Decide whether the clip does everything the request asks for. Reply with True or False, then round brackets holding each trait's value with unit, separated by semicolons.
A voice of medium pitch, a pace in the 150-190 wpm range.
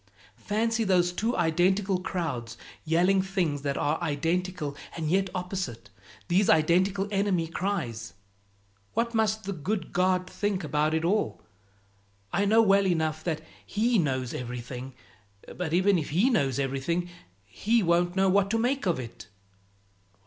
False (180 Hz; 140 wpm)